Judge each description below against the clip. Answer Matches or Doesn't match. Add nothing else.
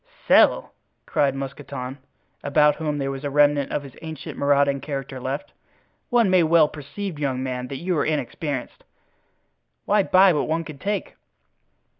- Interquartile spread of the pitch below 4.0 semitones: Matches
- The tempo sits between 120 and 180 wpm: Matches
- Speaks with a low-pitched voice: Doesn't match